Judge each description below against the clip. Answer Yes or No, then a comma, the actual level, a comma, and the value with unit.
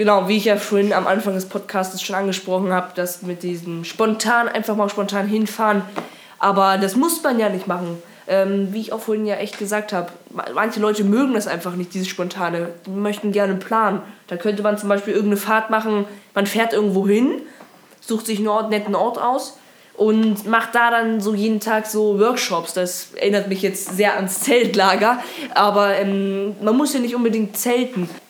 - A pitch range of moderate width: No, narrow, 2.2 semitones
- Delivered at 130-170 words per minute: No, fast, 190 wpm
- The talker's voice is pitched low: No, high, 205 Hz